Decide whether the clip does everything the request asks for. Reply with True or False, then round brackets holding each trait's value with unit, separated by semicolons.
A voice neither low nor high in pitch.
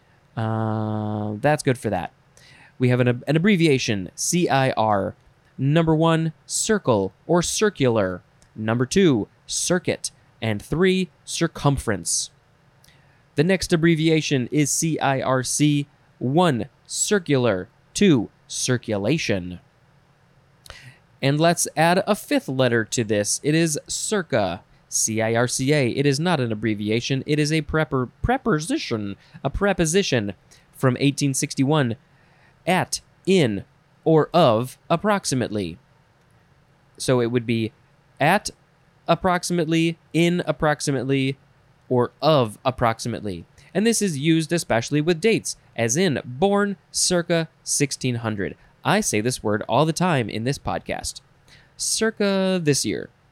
True (145 Hz)